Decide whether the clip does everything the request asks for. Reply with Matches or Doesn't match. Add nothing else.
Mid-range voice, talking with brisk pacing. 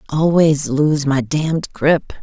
Doesn't match